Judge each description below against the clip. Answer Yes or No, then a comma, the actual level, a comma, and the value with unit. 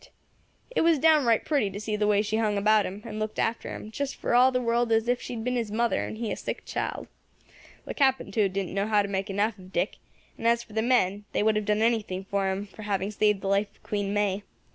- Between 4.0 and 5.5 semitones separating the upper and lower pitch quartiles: No, narrow, 2.6 semitones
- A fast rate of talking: Yes, fast, 260 wpm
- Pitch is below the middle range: No, high, 215 Hz